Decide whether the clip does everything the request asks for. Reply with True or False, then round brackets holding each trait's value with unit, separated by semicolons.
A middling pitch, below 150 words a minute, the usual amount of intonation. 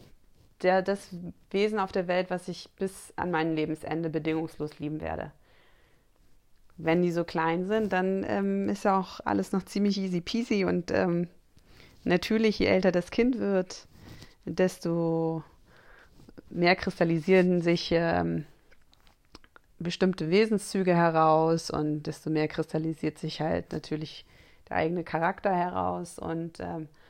True (175 Hz; 130 wpm; 3.2 semitones)